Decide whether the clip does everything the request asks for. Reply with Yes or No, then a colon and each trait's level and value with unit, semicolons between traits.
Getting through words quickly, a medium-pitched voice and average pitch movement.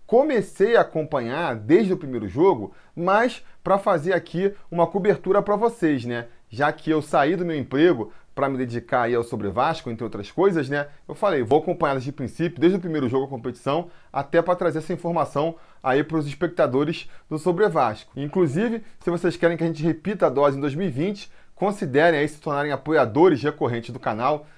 Yes: fast, 190 wpm; medium, 160 Hz; average, 4.6 semitones